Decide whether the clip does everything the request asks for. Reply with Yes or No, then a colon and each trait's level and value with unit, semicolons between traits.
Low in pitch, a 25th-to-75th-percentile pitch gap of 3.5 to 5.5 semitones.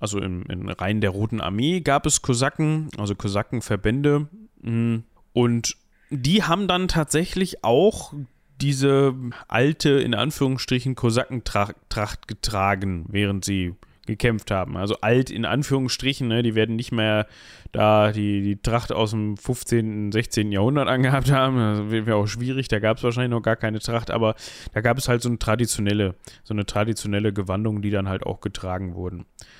Yes: low, 115 Hz; average, 4.1 semitones